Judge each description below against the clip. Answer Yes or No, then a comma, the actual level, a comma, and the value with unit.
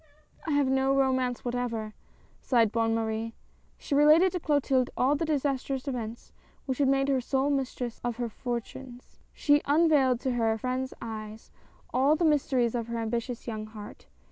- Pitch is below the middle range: No, very high, 255 Hz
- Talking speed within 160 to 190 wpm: Yes, average, 165 wpm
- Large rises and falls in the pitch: No, average, 3.1 semitones